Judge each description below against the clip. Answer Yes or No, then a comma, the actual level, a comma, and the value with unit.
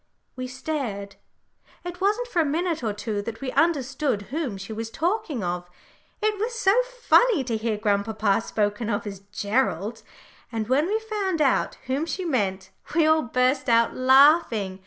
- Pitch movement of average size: No, wide, 7.7 semitones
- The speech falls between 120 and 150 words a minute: No, average, 165 wpm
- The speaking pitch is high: Yes, very high, 255 Hz